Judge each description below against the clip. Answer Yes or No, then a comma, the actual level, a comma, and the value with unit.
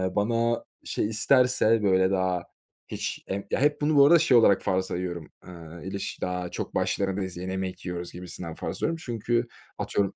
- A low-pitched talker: Yes, very low, 95 Hz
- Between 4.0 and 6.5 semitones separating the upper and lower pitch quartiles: Yes, average, 4.4 semitones